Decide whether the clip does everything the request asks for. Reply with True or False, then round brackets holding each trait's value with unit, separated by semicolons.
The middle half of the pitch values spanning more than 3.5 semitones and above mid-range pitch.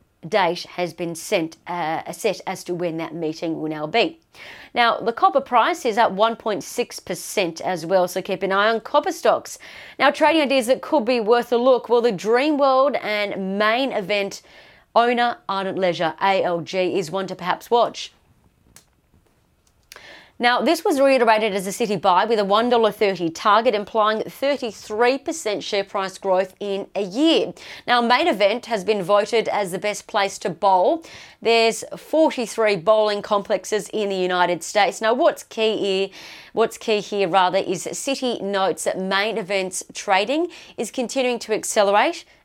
True (3.9 semitones; 215 Hz)